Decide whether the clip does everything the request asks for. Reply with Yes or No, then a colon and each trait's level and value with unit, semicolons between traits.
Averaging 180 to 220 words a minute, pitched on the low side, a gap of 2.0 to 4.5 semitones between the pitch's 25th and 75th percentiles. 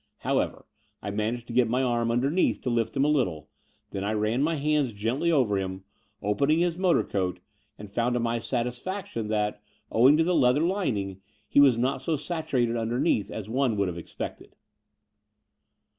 No: average, 185 wpm; low, 120 Hz; average, 5.1 semitones